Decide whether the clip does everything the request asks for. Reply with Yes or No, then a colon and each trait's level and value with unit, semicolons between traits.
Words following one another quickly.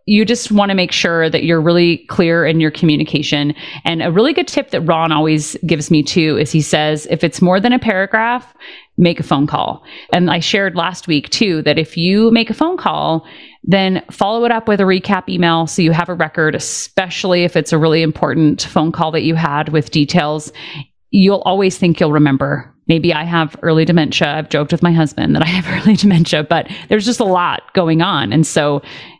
Yes: fast, 215 wpm